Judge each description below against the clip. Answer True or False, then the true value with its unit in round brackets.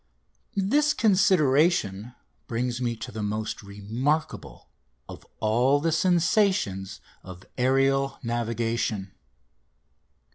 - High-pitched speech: False (125 Hz)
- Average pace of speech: False (85 wpm)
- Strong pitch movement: True (6.7 semitones)